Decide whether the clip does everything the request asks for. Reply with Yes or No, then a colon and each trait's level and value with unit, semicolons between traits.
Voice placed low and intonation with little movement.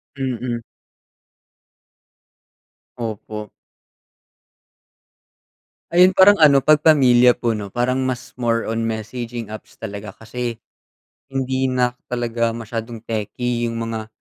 Yes: low, 120 Hz; narrow, 2.1 semitones